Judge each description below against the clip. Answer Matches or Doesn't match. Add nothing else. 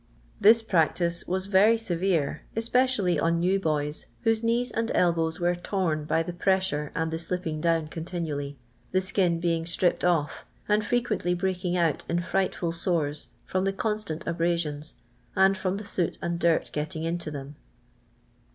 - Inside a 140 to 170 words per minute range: Matches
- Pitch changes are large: Doesn't match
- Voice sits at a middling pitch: Matches